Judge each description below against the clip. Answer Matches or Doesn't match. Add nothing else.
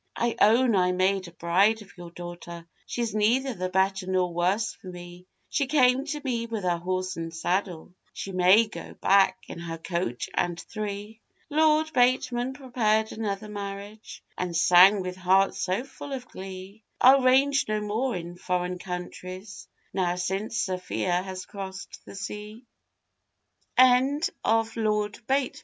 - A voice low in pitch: Doesn't match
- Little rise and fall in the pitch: Doesn't match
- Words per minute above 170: Doesn't match